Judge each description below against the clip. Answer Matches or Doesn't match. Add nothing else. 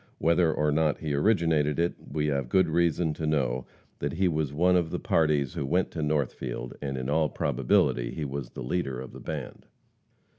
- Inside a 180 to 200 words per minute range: Matches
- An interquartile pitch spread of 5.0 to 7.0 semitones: Doesn't match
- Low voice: Matches